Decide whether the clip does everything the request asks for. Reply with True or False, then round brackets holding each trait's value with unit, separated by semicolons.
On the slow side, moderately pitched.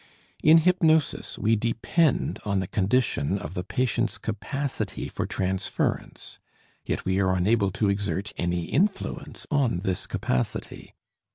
False (125 wpm; 105 Hz)